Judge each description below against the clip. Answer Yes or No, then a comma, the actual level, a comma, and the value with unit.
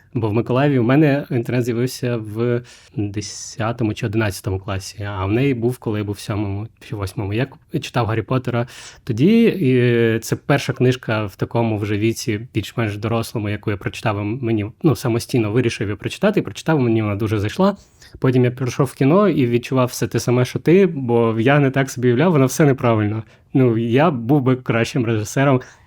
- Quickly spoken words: Yes, fast, 190 wpm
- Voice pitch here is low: Yes, low, 120 Hz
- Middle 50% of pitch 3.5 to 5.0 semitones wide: No, average, 2.8 semitones